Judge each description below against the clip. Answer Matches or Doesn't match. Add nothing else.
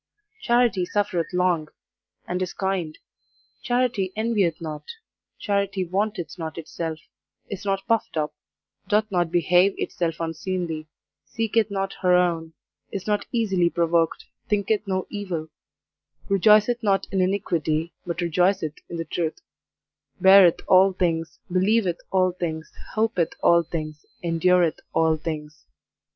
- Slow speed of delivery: Matches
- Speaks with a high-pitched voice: Doesn't match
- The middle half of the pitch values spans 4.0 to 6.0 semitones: Doesn't match